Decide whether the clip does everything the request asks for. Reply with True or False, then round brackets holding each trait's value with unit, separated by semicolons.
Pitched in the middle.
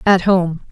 True (180 Hz)